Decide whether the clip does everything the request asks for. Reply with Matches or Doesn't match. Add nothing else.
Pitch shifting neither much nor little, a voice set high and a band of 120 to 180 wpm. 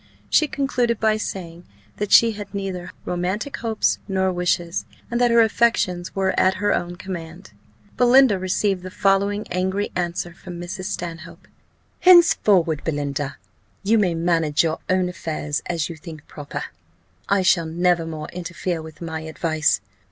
Doesn't match